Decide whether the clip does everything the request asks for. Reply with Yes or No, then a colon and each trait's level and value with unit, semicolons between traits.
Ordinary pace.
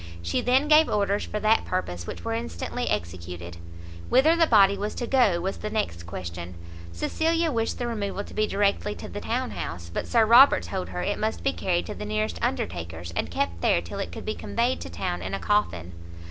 No: fast, 210 wpm